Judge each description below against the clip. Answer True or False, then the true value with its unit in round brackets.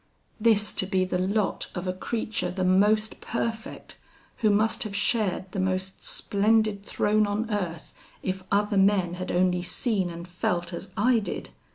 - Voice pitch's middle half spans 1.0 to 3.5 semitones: True (2.6 semitones)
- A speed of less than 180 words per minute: True (165 wpm)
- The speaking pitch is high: True (195 Hz)